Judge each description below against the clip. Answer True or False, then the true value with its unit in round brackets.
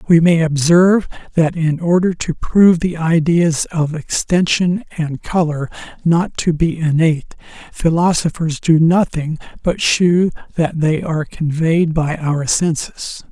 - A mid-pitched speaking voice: True (165 Hz)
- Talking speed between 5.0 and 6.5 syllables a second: False (4.1 syllables/s)